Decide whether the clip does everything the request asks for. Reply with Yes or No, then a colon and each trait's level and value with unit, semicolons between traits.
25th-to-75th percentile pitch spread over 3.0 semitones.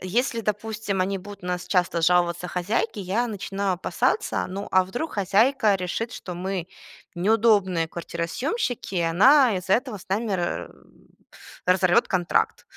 Yes: average, 3.6 semitones